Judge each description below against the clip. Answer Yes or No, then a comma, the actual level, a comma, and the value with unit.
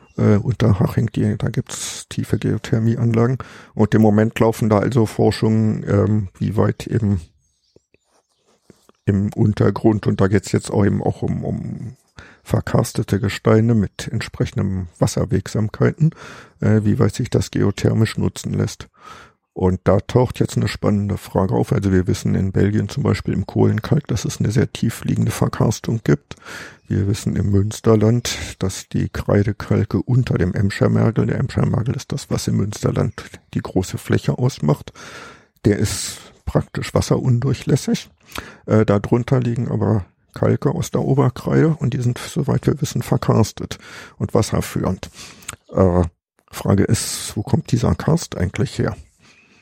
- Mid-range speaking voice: No, low, 110 Hz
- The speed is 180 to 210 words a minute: No, average, 145 wpm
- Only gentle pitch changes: No, average, 3.5 semitones